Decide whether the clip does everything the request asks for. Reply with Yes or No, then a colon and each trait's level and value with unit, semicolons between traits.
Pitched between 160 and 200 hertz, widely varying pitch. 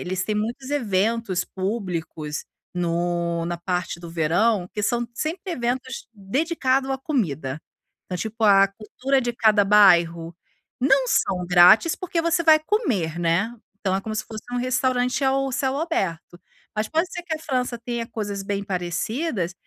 No: high, 215 Hz; wide, 6.6 semitones